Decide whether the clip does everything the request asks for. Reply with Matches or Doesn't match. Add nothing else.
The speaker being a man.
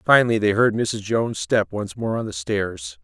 Matches